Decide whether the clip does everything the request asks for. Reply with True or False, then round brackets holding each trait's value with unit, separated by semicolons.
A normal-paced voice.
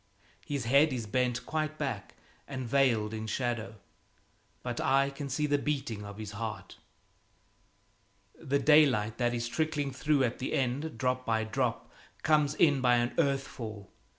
True (155 wpm)